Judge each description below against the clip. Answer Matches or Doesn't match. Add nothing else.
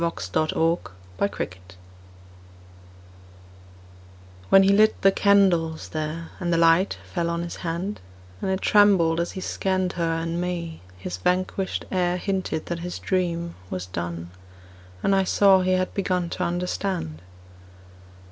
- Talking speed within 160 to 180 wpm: Doesn't match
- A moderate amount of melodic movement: Doesn't match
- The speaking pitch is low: Doesn't match